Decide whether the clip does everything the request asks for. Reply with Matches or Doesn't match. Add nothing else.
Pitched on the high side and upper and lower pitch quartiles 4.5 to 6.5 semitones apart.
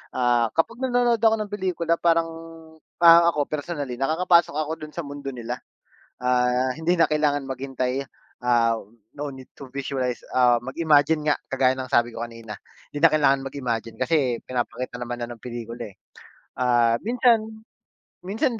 Doesn't match